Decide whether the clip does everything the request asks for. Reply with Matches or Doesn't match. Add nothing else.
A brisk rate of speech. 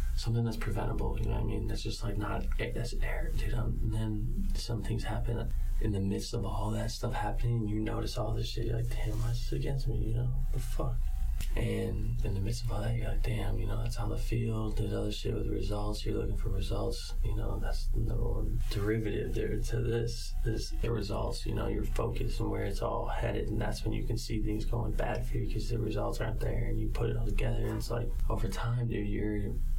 Matches